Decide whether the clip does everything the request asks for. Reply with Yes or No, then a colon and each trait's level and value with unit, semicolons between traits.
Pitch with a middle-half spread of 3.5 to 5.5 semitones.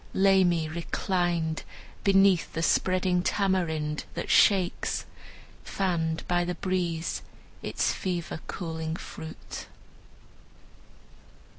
No: narrow, 2.5 semitones